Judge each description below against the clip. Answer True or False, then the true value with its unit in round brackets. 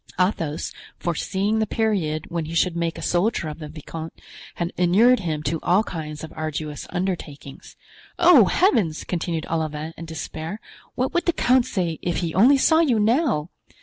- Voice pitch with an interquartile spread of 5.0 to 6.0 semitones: True (5.6 semitones)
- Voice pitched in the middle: True (170 Hz)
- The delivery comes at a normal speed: True (170 wpm)